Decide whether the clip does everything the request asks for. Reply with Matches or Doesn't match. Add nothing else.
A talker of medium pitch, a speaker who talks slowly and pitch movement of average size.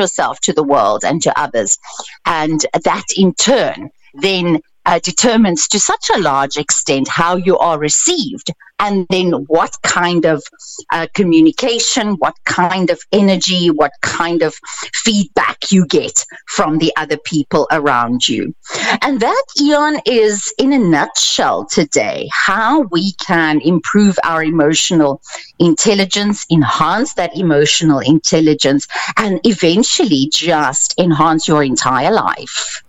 Matches